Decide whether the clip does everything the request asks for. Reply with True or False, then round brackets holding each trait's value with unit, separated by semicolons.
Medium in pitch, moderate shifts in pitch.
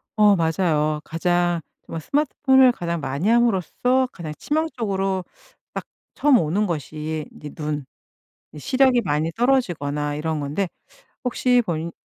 False (175 Hz; 7.8 semitones)